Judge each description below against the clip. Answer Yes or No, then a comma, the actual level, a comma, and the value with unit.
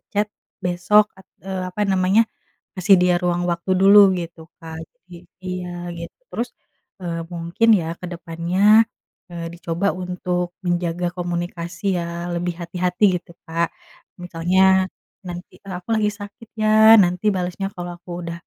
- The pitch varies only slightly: Yes, narrow, 1.7 semitones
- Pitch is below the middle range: No, medium, 180 Hz